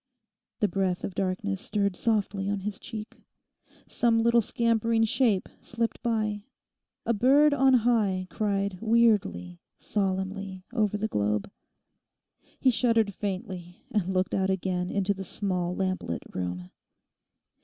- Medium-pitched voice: No, high, 200 Hz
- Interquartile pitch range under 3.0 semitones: No, average, 3.3 semitones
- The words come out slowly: Yes, slow, 125 wpm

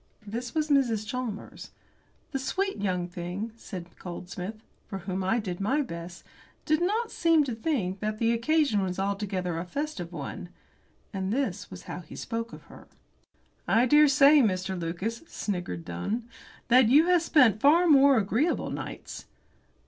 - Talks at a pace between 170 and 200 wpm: No, average, 155 wpm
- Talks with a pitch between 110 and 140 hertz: No, high, 220 Hz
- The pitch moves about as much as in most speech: No, wide, 7.1 semitones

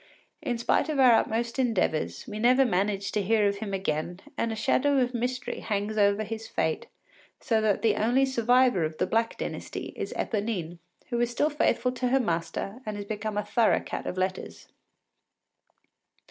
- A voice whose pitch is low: No, high, 220 Hz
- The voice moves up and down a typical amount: Yes, average, 3.5 semitones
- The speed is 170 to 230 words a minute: Yes, average, 180 wpm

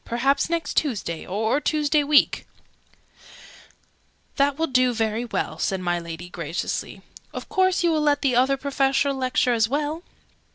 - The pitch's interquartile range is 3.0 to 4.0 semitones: No, average, 4.9 semitones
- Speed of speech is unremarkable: Yes, average, 155 wpm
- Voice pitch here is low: No, very high, 270 Hz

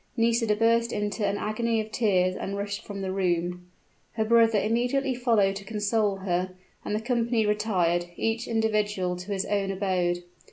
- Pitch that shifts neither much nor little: Yes, average, 3.0 semitones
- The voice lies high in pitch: Yes, high, 210 Hz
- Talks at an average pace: Yes, average, 165 wpm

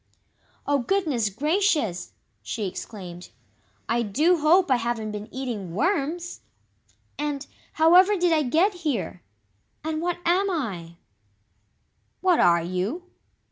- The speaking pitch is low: No, very high, 285 Hz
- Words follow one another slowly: Yes, slow, 115 wpm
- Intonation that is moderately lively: No, wide, 8.7 semitones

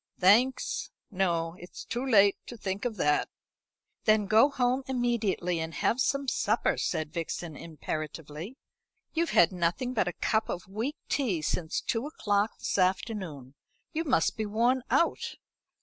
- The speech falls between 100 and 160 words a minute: Yes, average, 150 wpm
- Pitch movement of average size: No, wide, 6.1 semitones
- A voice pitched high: Yes, high, 205 Hz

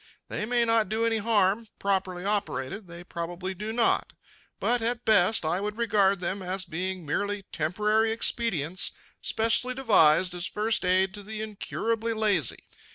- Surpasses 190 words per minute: No, average, 155 wpm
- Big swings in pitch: No, average, 3.4 semitones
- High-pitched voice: Yes, high, 205 Hz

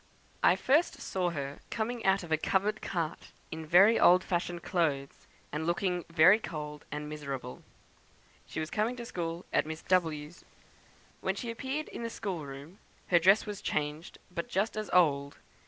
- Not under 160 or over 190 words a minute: Yes, average, 170 wpm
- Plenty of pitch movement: No, average, 4.7 semitones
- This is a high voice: No, medium, 175 Hz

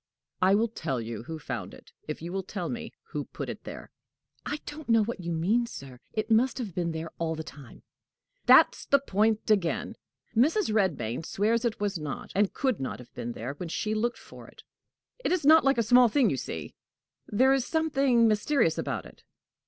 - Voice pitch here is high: Yes, high, 205 Hz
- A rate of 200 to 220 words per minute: Yes, fast, 205 wpm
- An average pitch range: No, wide, 6.9 semitones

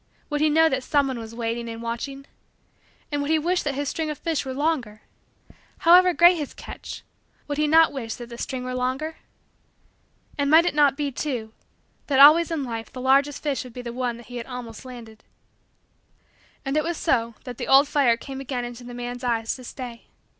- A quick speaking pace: Yes, fast, 210 wpm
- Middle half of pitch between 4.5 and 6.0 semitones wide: No, average, 3.7 semitones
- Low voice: No, very high, 265 Hz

